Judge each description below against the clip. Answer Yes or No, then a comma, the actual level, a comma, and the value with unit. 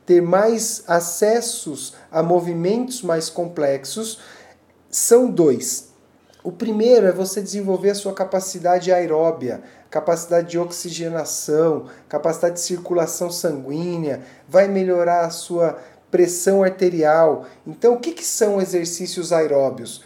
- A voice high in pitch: No, medium, 175 Hz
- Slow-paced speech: Yes, slow, 110 wpm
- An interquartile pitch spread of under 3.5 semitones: Yes, average, 2.9 semitones